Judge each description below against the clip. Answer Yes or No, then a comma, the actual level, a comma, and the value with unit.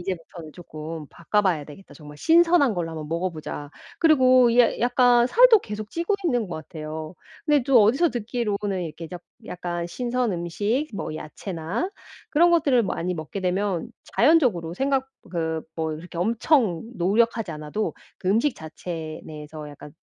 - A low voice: No, high, 190 Hz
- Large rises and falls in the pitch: Yes, wide, 7.3 semitones